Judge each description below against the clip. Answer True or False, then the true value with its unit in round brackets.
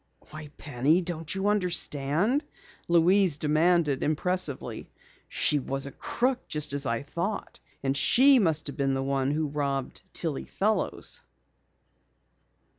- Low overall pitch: False (155 Hz)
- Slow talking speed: True (125 wpm)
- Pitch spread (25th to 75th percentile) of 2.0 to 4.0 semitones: False (4.5 semitones)